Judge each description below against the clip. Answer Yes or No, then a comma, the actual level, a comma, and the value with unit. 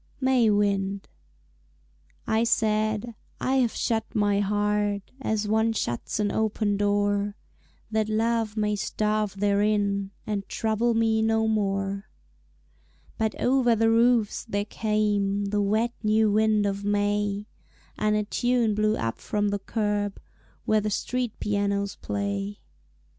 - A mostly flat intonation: Yes, narrow, 1.4 semitones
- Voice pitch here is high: Yes, high, 210 Hz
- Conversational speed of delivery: No, slow, 130 wpm